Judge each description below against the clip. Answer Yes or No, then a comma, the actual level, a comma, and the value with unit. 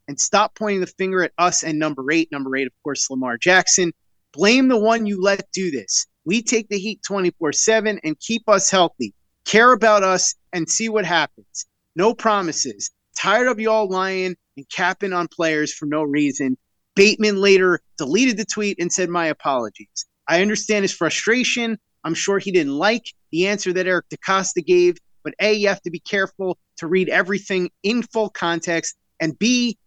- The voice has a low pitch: No, medium, 185 Hz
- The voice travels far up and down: No, average, 4.6 semitones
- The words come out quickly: No, average, 185 wpm